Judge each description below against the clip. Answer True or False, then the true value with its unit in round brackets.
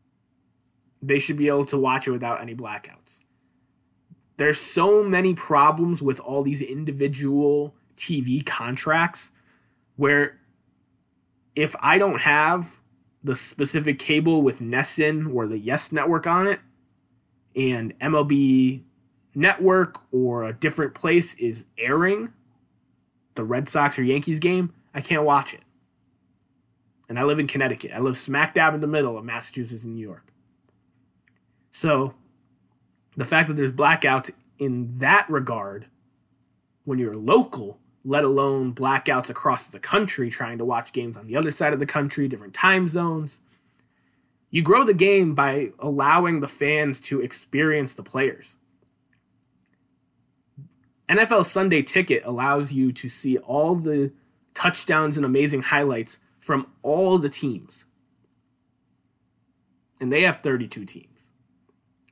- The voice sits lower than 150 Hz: True (140 Hz)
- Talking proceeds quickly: False (135 wpm)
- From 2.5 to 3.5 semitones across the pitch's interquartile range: True (3.2 semitones)